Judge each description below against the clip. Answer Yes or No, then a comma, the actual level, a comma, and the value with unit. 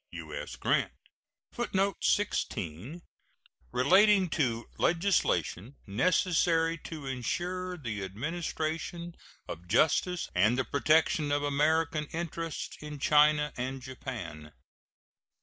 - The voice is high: No, medium, 150 Hz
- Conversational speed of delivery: No, slow, 95 wpm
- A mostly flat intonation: No, average, 5.2 semitones